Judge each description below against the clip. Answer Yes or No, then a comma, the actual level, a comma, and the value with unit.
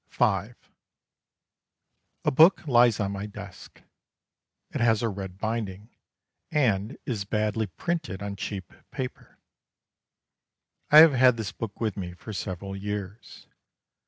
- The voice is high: No, low, 105 Hz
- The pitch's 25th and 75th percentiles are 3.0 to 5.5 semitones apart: Yes, average, 3.4 semitones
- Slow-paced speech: Yes, slow, 125 wpm